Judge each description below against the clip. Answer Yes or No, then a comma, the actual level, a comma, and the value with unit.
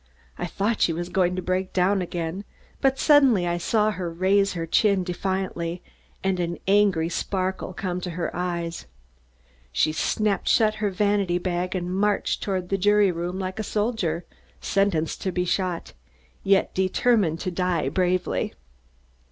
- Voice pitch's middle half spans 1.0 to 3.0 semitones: Yes, narrow, 2.4 semitones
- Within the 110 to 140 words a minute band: No, average, 155 wpm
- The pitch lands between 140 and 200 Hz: Yes, medium, 185 Hz